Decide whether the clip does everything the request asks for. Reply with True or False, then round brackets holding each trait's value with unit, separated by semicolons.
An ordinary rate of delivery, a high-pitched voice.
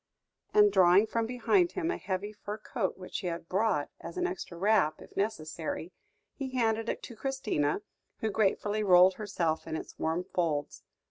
True (175 wpm; 205 Hz)